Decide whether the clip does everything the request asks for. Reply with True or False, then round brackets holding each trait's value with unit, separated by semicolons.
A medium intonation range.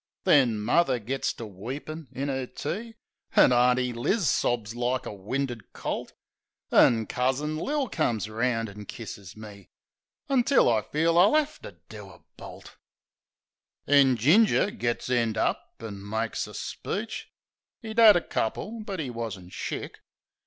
False (6.5 semitones)